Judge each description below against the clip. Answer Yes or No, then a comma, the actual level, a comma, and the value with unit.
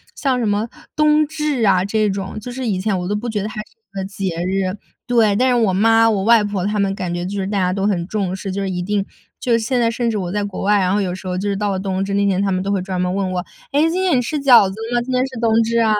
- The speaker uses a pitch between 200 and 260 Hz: Yes, high, 205 Hz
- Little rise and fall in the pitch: No, average, 3.2 semitones